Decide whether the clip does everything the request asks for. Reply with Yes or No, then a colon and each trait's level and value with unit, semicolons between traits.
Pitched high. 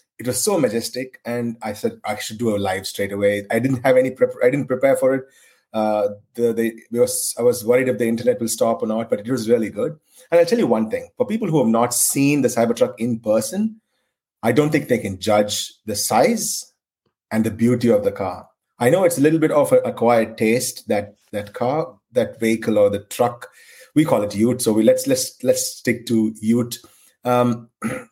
No: low, 120 Hz